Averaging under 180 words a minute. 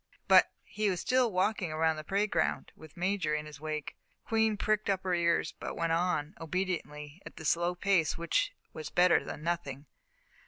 No: average, 185 wpm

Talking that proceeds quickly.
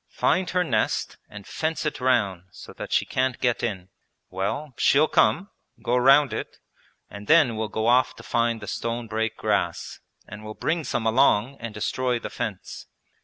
No: average, 175 wpm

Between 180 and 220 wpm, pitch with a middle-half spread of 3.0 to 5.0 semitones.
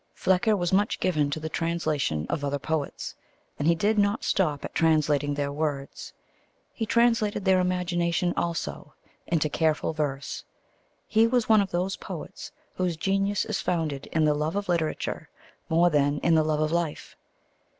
No: average, 165 wpm; average, 3.9 semitones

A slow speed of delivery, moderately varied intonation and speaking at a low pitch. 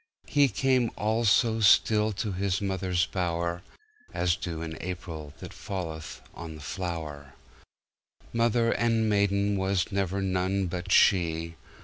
Yes: slow, 105 wpm; average, 3.9 semitones; very low, 95 Hz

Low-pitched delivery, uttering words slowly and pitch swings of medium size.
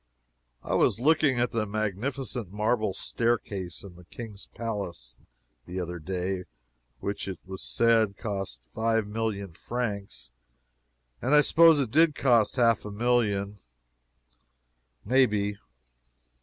Yes: low, 105 Hz; slow, 125 wpm; average, 3.6 semitones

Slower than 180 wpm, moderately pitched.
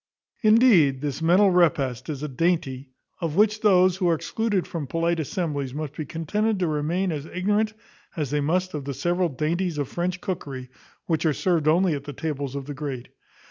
No: average, 190 wpm; medium, 160 Hz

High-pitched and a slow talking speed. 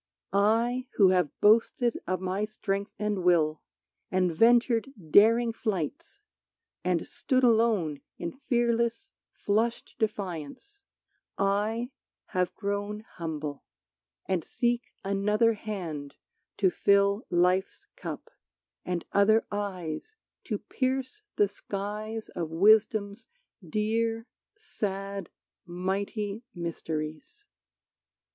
Yes: high, 205 Hz; slow, 95 wpm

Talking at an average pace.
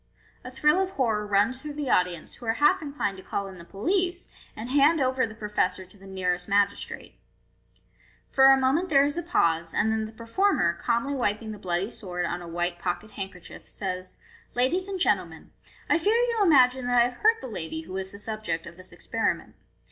No: fast, 210 wpm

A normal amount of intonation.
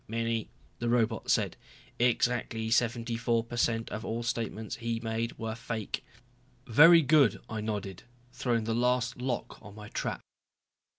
No: narrow, 1.3 semitones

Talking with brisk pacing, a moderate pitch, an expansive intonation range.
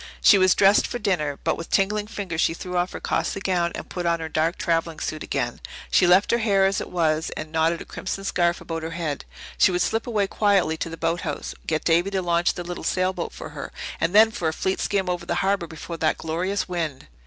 No: fast, 235 wpm; medium, 175 Hz; average, 2.9 semitones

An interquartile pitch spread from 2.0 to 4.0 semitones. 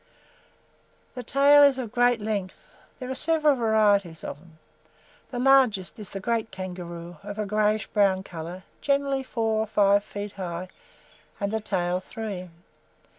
No: average, 4.6 semitones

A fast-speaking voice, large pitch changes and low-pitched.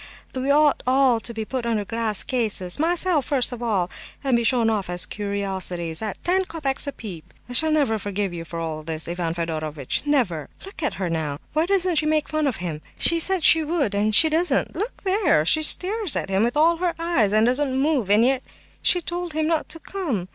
No: fast, 210 wpm; wide, 8.2 semitones; high, 245 Hz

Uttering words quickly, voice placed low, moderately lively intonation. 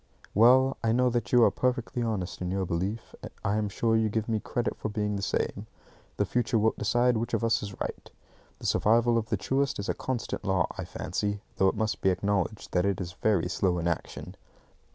Yes: fast, 215 wpm; low, 110 Hz; average, 3.2 semitones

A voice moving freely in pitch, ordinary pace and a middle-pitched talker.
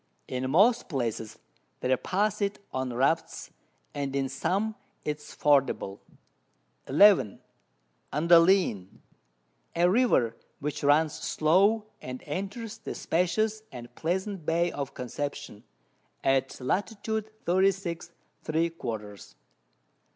No: wide, 6.5 semitones; slow, 105 wpm; medium, 155 Hz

